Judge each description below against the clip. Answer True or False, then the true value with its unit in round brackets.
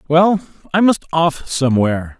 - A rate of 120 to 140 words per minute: True (135 wpm)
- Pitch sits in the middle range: True (155 Hz)